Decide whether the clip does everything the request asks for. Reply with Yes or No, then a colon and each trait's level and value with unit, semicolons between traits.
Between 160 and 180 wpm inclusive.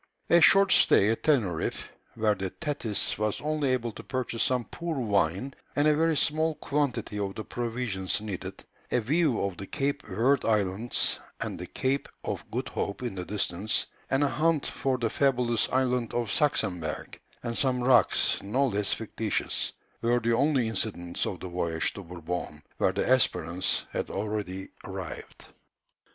Yes: average, 165 wpm